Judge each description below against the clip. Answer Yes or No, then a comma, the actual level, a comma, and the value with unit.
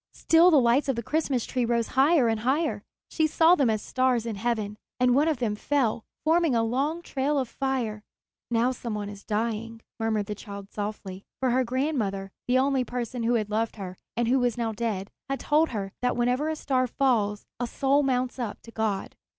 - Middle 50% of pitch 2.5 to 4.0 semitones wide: Yes, average, 3.6 semitones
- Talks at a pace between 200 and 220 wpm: Yes, fast, 205 wpm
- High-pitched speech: Yes, high, 240 Hz